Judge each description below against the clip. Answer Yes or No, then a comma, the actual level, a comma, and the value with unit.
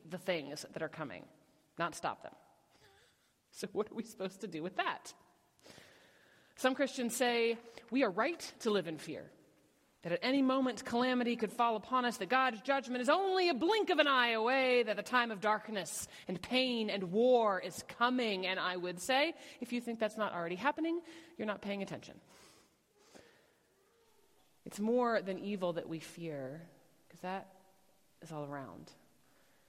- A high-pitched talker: Yes, high, 225 Hz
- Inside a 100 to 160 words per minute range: No, average, 170 wpm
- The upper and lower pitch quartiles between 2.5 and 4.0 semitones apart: No, wide, 5.4 semitones